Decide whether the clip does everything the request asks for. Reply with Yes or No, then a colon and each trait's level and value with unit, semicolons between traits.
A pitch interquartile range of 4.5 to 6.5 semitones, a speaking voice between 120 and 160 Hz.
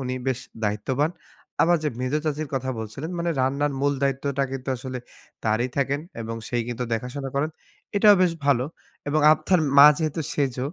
No: average, 3.0 semitones; low, 135 Hz